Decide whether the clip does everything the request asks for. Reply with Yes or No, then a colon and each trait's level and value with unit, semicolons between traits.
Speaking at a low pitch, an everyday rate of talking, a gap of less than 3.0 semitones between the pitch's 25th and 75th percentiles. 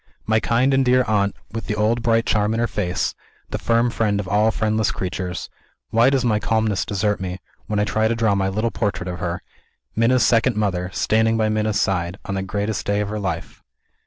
No: low, 105 Hz; fast, 215 wpm; narrow, 2.4 semitones